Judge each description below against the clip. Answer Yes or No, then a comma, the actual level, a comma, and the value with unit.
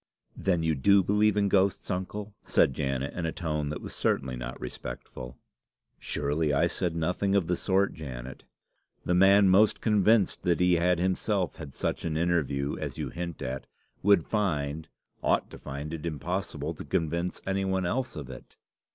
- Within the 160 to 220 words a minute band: Yes, average, 175 wpm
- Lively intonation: No, average, 4.7 semitones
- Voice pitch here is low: Yes, very low, 85 Hz